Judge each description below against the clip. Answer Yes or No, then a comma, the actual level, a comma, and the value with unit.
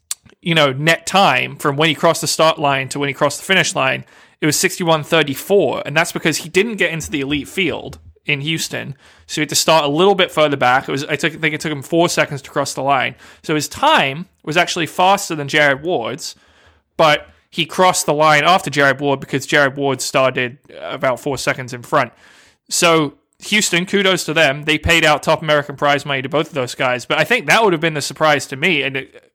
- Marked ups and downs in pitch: No, average, 2.9 semitones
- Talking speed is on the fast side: Yes, fast, 235 wpm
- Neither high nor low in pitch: Yes, medium, 155 Hz